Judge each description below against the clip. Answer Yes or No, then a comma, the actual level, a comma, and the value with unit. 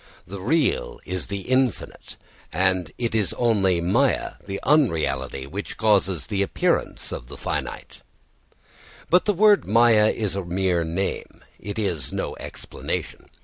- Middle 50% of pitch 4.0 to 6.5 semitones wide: Yes, average, 4.4 semitones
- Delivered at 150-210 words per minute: No, average, 140 wpm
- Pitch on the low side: Yes, low, 100 Hz